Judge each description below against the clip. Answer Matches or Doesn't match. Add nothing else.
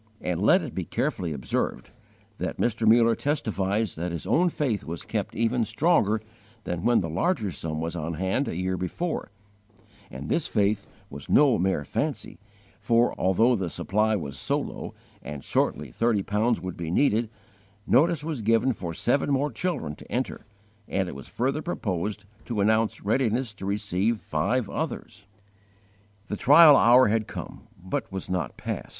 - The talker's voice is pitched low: Matches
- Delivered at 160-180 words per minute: Matches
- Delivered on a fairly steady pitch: Doesn't match